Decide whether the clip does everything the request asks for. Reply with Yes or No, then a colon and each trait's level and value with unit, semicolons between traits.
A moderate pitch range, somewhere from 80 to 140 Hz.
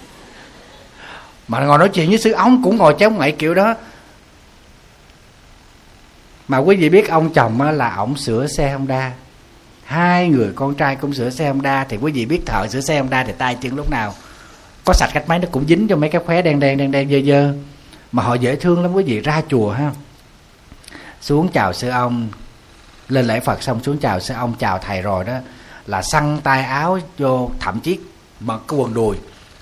Yes: average, 4.5 semitones; low, 135 Hz